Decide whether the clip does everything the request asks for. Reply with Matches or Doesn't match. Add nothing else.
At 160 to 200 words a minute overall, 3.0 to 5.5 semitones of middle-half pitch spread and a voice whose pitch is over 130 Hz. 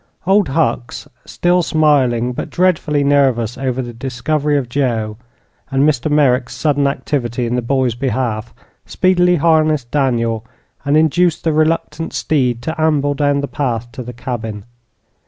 Doesn't match